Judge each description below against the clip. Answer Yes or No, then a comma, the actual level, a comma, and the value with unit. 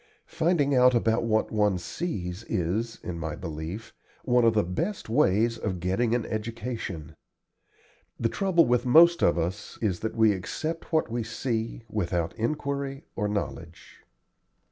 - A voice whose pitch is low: Yes, low, 110 Hz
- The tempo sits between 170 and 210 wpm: No, average, 145 wpm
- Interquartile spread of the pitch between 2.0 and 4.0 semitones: No, wide, 5.4 semitones